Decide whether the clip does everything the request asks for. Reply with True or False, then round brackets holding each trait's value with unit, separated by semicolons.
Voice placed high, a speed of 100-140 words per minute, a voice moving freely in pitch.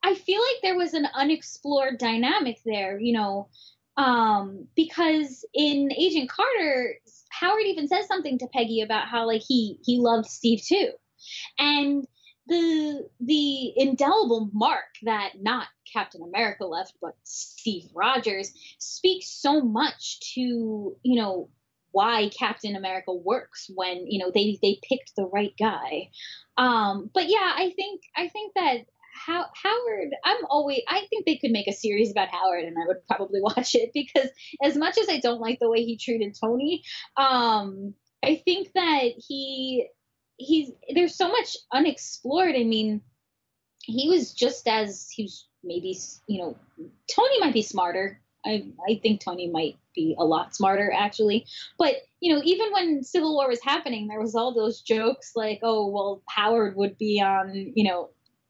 False (245 Hz; 165 wpm; 6.9 semitones)